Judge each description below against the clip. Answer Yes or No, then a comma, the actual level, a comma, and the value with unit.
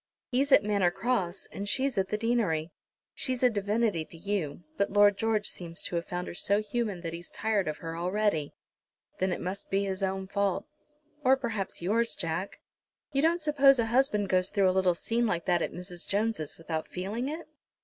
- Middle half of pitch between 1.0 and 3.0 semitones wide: No, average, 4.2 semitones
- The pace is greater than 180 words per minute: Yes, average, 200 wpm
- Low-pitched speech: No, high, 200 Hz